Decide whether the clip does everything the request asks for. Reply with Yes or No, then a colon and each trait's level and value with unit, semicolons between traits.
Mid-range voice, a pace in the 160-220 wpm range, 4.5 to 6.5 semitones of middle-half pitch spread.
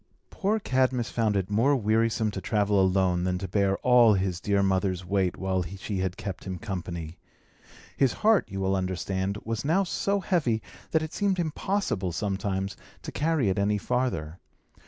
No: low, 100 Hz; average, 170 wpm; average, 5.0 semitones